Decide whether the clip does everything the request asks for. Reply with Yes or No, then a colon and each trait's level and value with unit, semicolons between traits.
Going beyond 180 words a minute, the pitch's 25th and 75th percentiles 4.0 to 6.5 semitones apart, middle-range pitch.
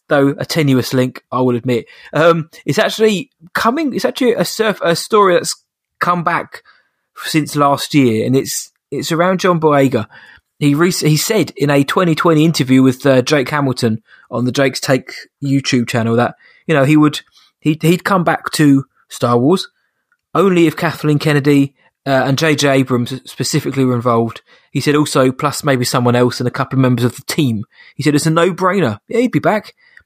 Yes: average, 190 wpm; average, 4.5 semitones; medium, 145 Hz